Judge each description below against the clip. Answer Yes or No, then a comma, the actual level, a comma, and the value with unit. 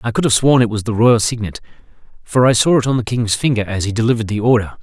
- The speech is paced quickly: Yes, fast, 275 wpm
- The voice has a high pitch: No, low, 115 Hz